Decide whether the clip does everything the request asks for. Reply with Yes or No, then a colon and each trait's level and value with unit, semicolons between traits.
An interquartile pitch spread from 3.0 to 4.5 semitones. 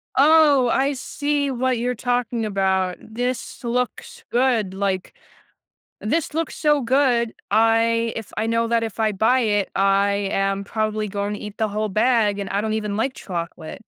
Yes: average, 3.7 semitones